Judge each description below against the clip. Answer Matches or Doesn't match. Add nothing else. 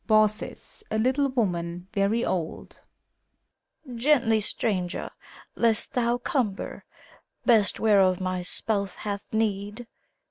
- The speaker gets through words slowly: Matches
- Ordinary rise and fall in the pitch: Matches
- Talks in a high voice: Matches